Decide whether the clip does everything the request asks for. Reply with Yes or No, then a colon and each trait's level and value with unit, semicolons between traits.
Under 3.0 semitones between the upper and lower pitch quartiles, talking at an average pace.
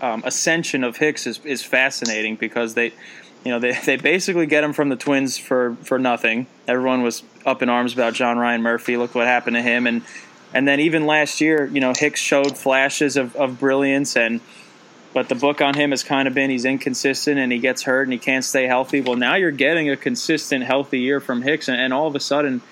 No: narrow, 2.5 semitones; fast, 230 wpm